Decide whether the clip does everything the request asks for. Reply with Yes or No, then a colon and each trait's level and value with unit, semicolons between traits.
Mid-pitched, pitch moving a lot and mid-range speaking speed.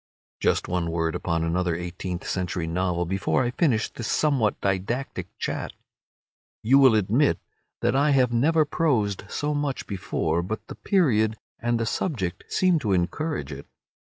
No: low, 110 Hz; wide, 7.3 semitones; average, 155 wpm